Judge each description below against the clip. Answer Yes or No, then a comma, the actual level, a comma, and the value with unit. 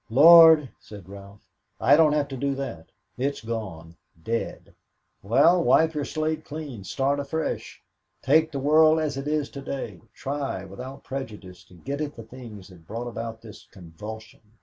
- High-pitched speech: No, low, 135 Hz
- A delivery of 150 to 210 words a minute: Yes, average, 165 wpm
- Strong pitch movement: Yes, wide, 5.8 semitones